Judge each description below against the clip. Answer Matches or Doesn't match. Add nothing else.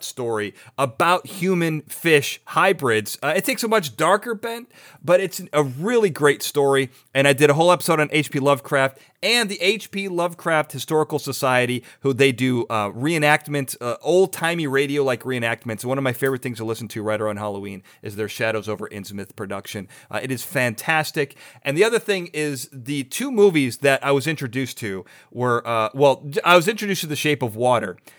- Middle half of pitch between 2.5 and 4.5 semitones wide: Doesn't match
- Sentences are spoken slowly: Doesn't match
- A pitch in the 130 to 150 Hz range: Matches